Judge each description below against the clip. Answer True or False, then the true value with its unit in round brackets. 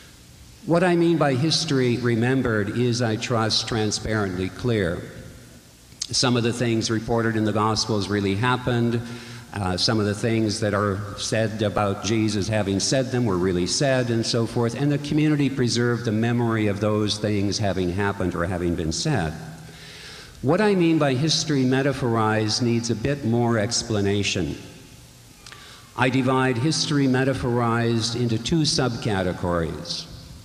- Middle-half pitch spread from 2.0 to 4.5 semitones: True (3.5 semitones)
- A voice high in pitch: False (115 Hz)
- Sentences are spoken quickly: False (145 wpm)